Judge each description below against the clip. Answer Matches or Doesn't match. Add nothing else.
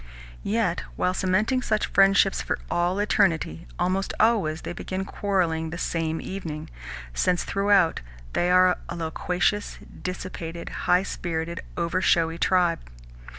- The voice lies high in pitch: Doesn't match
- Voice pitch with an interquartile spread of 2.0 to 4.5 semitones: Matches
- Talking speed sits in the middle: Doesn't match